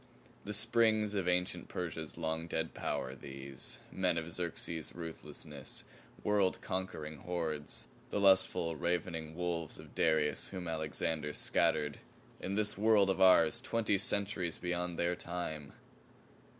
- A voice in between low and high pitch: No, very low, 85 Hz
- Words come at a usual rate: No, slow, 125 wpm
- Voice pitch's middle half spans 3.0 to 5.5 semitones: Yes, average, 3.3 semitones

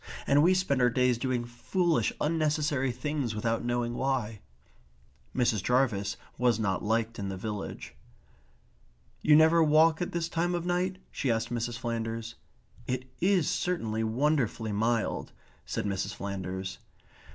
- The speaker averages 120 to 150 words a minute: Yes, average, 140 wpm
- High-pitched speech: No, low, 120 Hz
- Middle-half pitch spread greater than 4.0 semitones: Yes, wide, 5.5 semitones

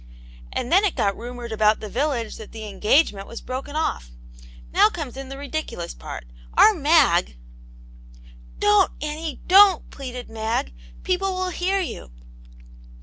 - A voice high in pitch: Yes, very high, 250 Hz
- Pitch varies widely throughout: Yes, wide, 7.1 semitones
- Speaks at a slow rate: No, average, 150 wpm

